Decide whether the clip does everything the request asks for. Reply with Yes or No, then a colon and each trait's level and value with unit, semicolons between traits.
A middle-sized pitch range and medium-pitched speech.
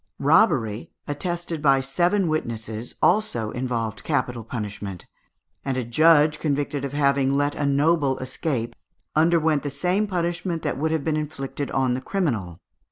Yes: average, 4.3 semitones; medium, 145 Hz